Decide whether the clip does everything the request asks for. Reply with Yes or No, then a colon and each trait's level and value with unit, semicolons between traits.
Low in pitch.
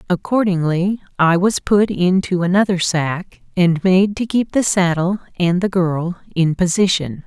No: medium, 180 Hz